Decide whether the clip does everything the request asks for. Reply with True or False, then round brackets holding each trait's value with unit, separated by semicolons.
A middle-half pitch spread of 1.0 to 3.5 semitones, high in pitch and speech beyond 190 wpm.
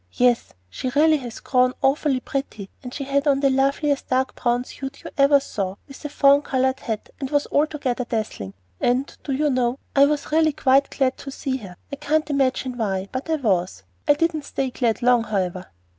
True (2.7 semitones; 265 Hz; 200 wpm)